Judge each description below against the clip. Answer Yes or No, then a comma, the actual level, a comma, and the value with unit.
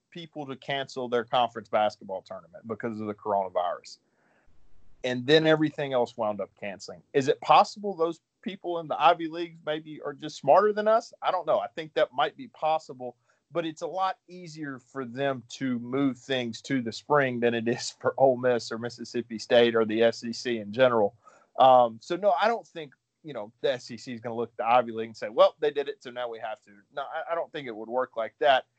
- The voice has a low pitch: Yes, low, 130 Hz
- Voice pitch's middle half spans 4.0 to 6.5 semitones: Yes, average, 5.2 semitones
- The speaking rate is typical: No, fast, 225 wpm